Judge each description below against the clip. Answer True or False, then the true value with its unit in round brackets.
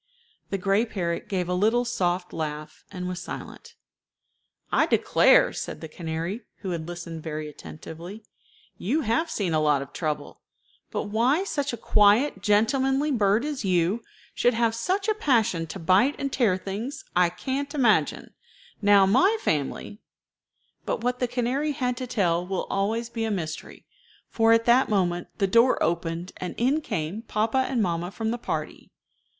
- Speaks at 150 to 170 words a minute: True (165 wpm)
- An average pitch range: False (5.8 semitones)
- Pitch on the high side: True (205 Hz)